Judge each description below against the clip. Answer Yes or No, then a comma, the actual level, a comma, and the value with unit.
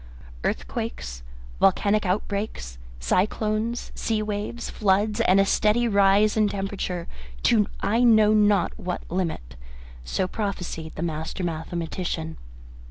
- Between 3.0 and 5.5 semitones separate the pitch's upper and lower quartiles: Yes, average, 3.8 semitones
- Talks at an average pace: No, slow, 110 wpm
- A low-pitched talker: No, high, 195 Hz